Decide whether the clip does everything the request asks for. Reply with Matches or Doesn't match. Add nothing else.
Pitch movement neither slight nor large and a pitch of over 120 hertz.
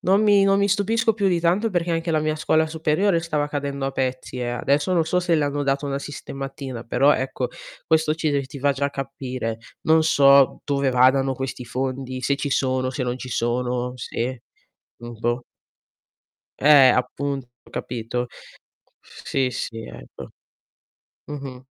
Matches